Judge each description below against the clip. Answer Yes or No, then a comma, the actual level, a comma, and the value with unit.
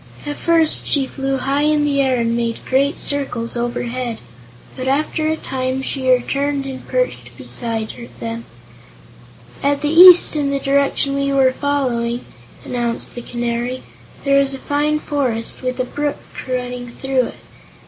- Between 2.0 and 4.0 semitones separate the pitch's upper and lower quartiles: Yes, narrow, 2.6 semitones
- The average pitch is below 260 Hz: No, very high, 270 Hz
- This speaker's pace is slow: No, average, 155 wpm